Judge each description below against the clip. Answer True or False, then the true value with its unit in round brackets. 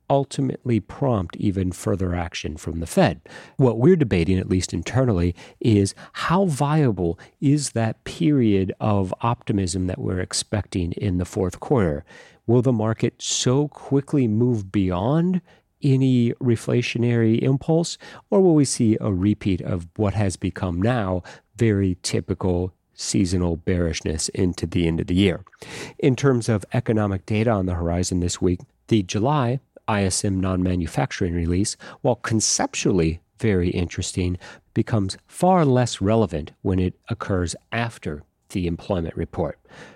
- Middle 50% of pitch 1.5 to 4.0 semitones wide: False (5.2 semitones)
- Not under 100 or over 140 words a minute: True (135 wpm)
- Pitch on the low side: True (105 Hz)